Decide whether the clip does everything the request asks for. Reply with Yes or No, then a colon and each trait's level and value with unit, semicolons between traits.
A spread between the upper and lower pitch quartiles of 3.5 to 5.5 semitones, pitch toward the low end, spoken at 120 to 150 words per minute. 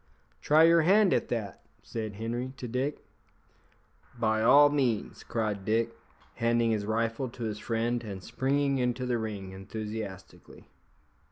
No: average, 2.9 semitones; low, 115 Hz; average, 140 wpm